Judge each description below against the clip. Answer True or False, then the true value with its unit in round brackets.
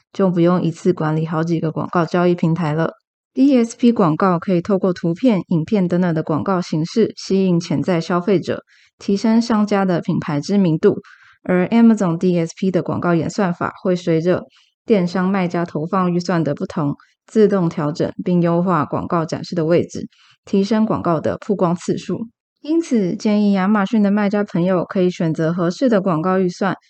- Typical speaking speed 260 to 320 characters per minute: True (290 characters per minute)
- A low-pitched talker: False (180 Hz)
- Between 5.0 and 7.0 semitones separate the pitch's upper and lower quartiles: False (3.1 semitones)